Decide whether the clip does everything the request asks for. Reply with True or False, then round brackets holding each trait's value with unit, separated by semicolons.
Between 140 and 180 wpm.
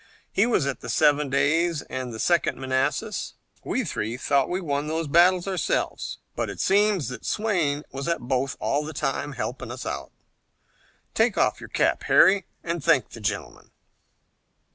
True (165 wpm)